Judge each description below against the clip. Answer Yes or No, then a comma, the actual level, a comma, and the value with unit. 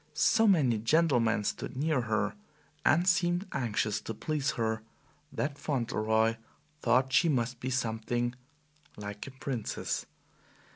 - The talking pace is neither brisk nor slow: No, slow, 125 wpm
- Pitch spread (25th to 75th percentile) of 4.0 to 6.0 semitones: Yes, average, 4.9 semitones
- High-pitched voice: No, low, 125 Hz